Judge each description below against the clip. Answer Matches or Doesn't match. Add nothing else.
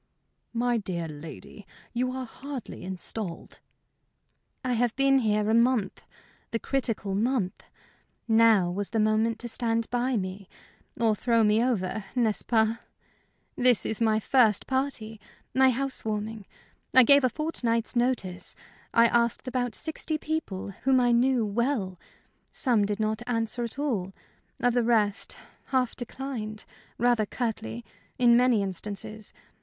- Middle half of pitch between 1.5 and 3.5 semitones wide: Matches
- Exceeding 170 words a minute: Doesn't match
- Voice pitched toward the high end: Matches